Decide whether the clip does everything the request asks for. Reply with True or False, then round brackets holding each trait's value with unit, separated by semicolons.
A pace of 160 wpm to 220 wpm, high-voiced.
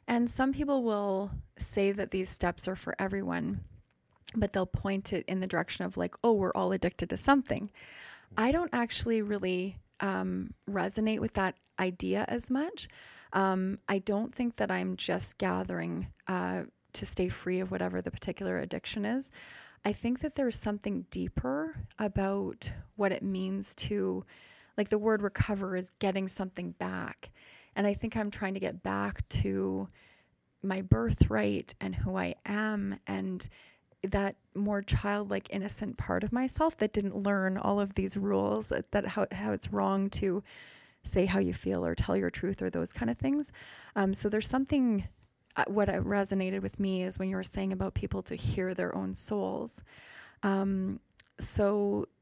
True (170 wpm; 195 Hz)